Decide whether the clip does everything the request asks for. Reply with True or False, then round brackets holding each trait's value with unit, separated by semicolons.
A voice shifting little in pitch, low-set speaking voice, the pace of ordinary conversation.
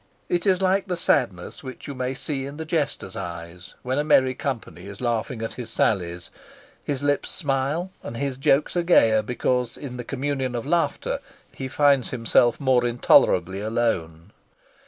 False (4.2 semitones; 130 Hz; 170 wpm)